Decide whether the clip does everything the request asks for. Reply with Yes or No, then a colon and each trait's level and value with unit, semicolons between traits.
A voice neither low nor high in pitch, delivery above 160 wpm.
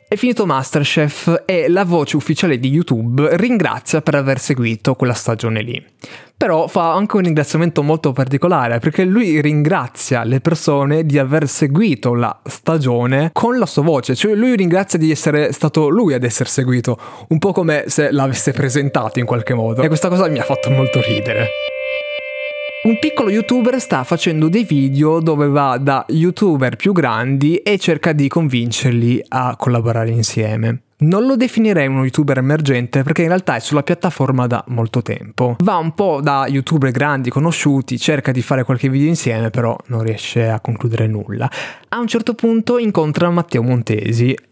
Yes: medium, 145 Hz; fast, 170 wpm